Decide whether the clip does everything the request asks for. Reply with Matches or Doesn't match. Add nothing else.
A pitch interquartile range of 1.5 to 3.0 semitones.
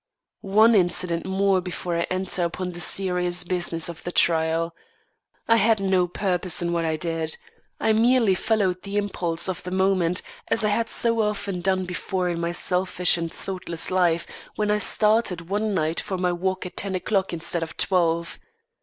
Matches